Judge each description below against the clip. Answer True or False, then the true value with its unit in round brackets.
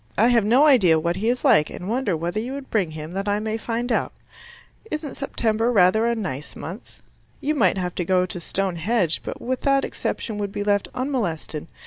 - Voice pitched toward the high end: True (210 Hz)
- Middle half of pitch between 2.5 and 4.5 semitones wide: False (5.2 semitones)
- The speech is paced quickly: True (210 wpm)